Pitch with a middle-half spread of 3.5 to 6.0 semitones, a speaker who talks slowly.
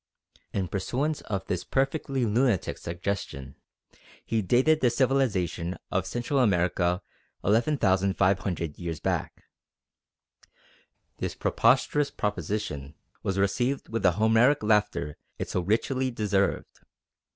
Yes: wide, 5.5 semitones; slow, 105 wpm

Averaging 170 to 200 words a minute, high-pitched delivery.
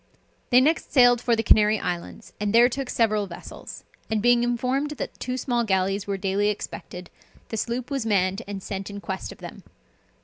Yes: average, 190 wpm; high, 220 Hz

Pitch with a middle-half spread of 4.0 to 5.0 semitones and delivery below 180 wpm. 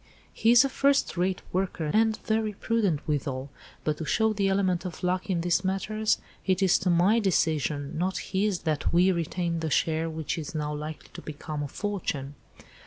No: average, 4.3 semitones; average, 185 wpm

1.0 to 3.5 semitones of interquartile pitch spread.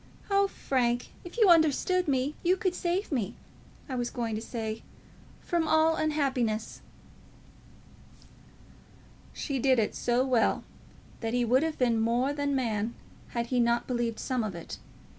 No: average, 4.9 semitones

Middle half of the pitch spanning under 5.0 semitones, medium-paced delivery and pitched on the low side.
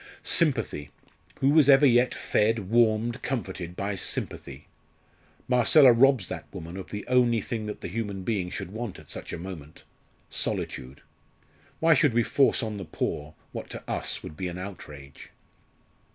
No: average, 5.3 semitones; average, 160 wpm; low, 110 Hz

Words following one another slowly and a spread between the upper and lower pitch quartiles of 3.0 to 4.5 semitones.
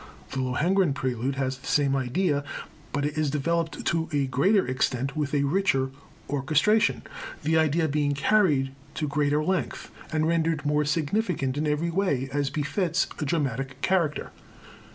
No: average, 155 wpm; average, 3.3 semitones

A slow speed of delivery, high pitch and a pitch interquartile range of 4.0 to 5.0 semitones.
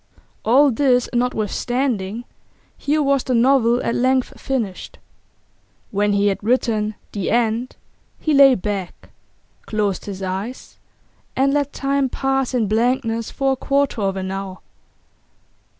Yes: slow, 130 wpm; high, 240 Hz; average, 4.5 semitones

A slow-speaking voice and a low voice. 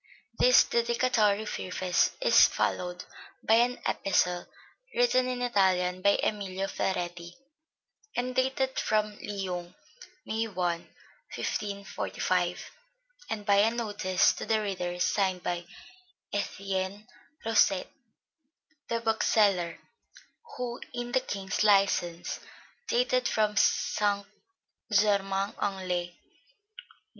No: slow, 100 wpm; high, 200 Hz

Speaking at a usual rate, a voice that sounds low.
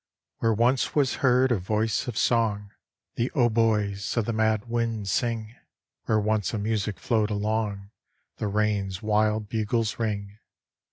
Yes: average, 145 wpm; low, 110 Hz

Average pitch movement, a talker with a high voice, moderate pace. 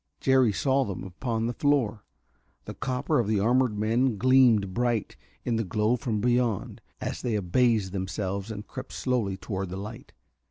No: average, 3.8 semitones; low, 115 Hz; average, 165 wpm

